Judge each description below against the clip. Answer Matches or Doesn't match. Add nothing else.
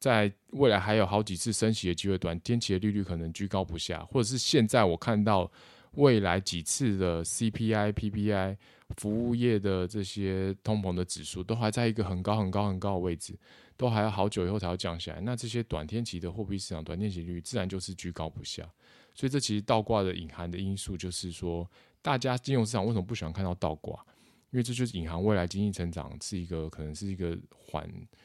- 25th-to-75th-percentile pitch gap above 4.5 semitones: Doesn't match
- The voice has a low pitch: Matches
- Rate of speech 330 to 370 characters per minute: Matches